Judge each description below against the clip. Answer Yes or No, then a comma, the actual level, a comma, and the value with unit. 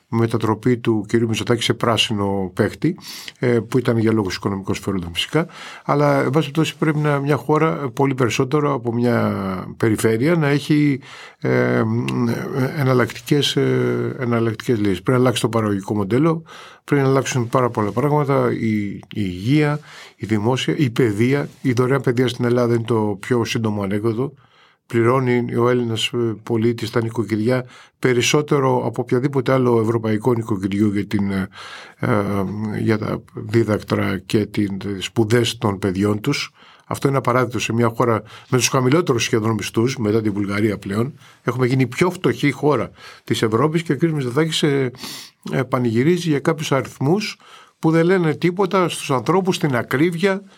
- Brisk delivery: No, average, 145 wpm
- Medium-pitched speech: No, low, 120 Hz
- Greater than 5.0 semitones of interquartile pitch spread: No, average, 4.2 semitones